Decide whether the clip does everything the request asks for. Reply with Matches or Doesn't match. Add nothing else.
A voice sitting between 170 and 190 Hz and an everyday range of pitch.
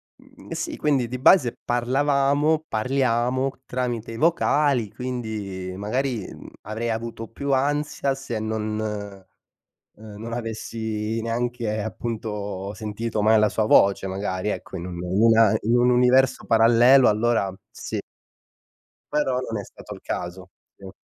Doesn't match